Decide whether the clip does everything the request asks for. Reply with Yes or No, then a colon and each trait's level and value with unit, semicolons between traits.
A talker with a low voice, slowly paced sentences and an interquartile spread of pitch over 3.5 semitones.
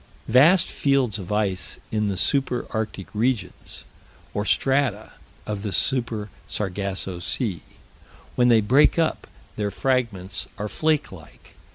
Yes: low, 110 Hz; slow, 130 wpm; average, 4.6 semitones